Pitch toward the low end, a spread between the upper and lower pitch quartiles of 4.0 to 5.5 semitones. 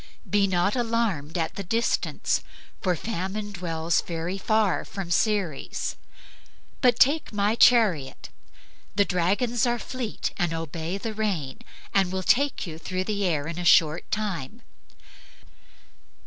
No: high, 195 Hz; average, 4.4 semitones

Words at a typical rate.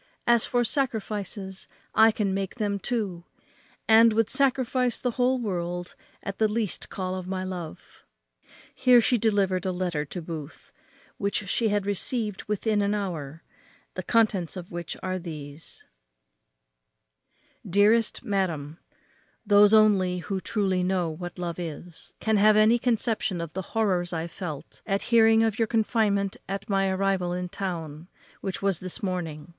Yes: average, 150 wpm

